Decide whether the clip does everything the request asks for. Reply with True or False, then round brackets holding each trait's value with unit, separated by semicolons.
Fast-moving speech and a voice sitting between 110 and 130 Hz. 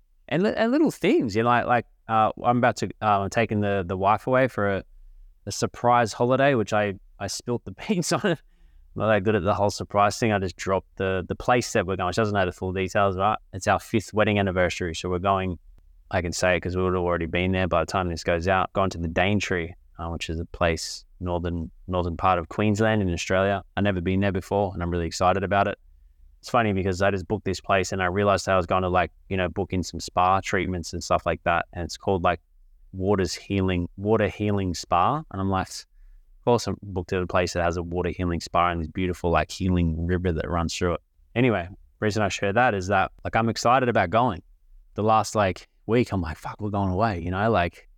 False (245 wpm; 95 Hz)